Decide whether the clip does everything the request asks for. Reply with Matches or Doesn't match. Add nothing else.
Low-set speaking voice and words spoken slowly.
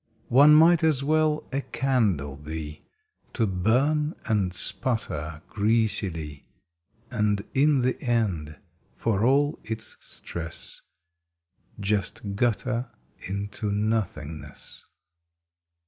Matches